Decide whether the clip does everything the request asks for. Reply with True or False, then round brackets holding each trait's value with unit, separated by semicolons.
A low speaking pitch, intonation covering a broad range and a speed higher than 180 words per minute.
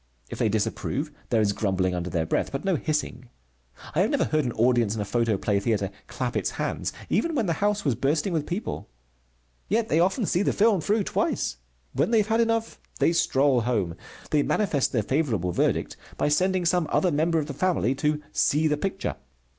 False (150 Hz; 8.3 semitones; 200 wpm)